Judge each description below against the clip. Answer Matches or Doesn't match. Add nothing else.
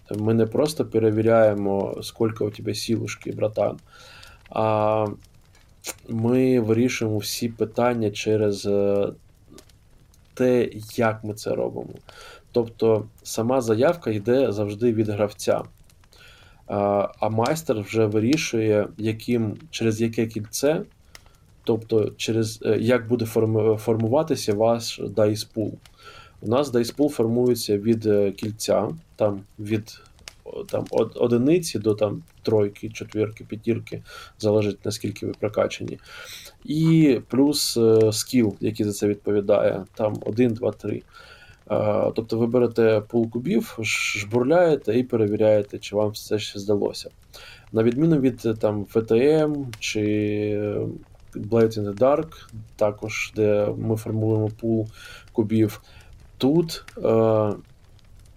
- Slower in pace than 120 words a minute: Matches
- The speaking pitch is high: Doesn't match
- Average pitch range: Doesn't match